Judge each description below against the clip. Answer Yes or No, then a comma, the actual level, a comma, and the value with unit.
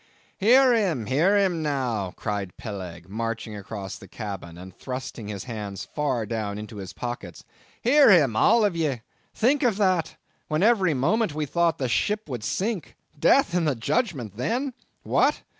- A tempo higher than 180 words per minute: No, average, 160 wpm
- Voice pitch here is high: No, low, 135 Hz